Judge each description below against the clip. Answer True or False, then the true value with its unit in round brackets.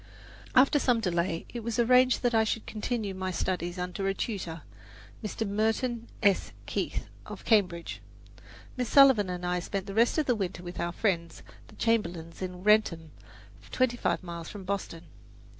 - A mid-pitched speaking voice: False (200 Hz)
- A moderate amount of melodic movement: True (4.5 semitones)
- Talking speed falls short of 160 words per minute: False (165 wpm)